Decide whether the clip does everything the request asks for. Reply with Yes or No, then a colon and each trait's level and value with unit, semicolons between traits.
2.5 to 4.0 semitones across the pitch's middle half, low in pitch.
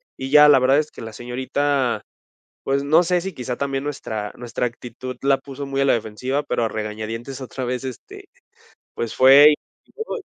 Yes: average, 2.8 semitones; low, 130 Hz